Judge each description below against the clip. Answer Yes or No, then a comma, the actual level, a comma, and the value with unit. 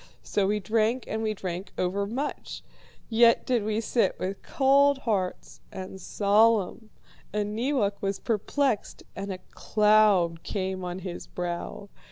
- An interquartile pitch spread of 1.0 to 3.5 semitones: Yes, average, 3.2 semitones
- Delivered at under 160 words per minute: Yes, slow, 135 wpm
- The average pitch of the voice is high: Yes, high, 205 Hz